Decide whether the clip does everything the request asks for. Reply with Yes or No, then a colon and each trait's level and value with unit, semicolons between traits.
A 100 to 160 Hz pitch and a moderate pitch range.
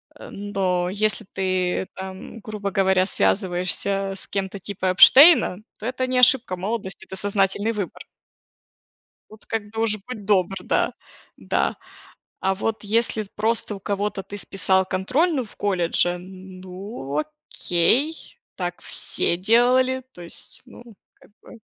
No: high, 200 Hz; average, 3.1 semitones